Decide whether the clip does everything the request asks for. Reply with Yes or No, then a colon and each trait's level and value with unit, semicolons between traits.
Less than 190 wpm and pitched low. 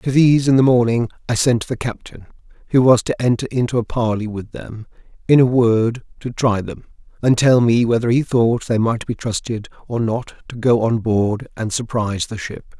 No: fast, 205 wpm; low, 115 Hz